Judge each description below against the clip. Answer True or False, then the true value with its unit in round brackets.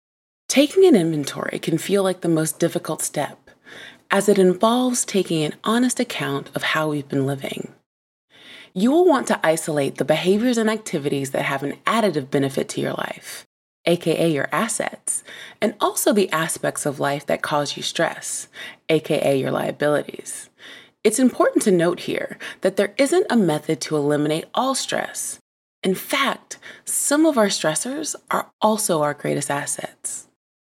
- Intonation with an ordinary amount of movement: False (6.5 semitones)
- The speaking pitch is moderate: True (175 Hz)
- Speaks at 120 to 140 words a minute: False (155 wpm)